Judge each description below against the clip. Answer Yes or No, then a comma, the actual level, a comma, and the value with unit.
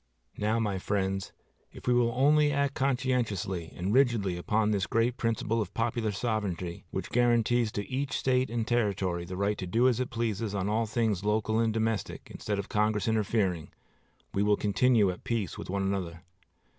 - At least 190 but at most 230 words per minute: No, average, 180 wpm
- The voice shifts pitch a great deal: No, average, 3.2 semitones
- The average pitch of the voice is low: Yes, low, 110 Hz